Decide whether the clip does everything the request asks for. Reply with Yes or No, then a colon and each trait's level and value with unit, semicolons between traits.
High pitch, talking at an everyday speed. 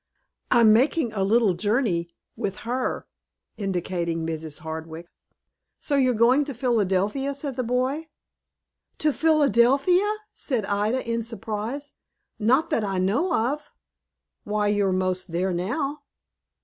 No: high, 230 Hz; slow, 125 wpm